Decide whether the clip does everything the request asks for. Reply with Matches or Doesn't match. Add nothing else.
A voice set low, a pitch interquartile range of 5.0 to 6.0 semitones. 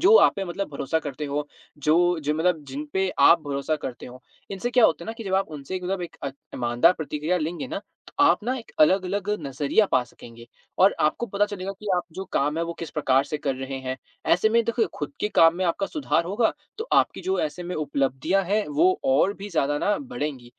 Doesn't match